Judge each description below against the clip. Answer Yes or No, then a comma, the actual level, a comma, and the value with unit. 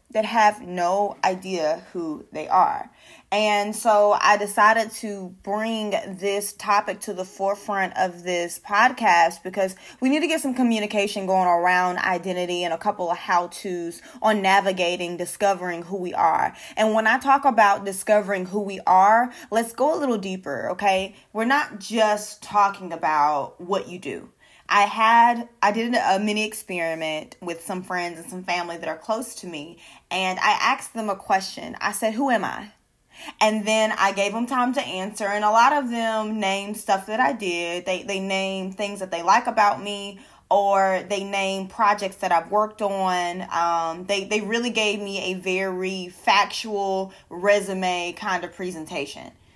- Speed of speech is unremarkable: Yes, average, 175 wpm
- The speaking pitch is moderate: No, high, 200 Hz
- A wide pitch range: No, average, 2.8 semitones